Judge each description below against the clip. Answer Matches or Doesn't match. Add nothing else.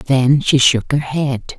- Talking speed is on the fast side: Doesn't match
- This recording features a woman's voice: Matches